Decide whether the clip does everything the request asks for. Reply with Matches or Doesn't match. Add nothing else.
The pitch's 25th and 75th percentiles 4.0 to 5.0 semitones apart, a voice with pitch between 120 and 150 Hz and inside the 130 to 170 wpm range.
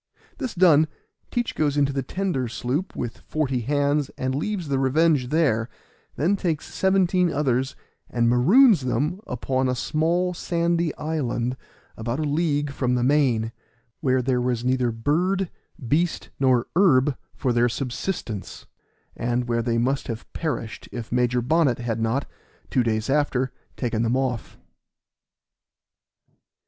Matches